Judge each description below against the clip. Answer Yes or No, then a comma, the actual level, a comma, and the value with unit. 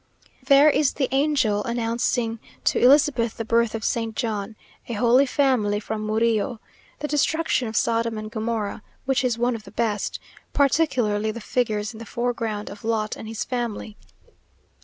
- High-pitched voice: Yes, high, 230 Hz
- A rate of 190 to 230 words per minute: No, average, 160 wpm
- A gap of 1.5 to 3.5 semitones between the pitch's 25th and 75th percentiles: Yes, average, 2.7 semitones